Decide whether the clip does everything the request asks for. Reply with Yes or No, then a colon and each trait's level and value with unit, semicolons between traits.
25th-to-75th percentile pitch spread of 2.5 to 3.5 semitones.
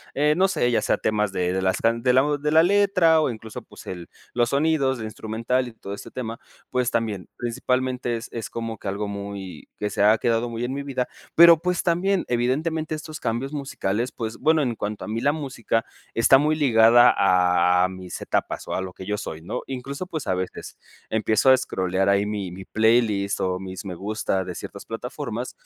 No: average, 5.2 semitones